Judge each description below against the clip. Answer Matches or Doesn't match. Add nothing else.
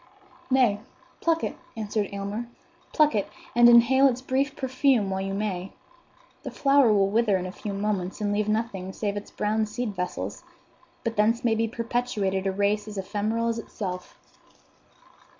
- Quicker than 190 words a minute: Doesn't match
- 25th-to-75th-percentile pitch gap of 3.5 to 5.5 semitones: Doesn't match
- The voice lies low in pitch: Doesn't match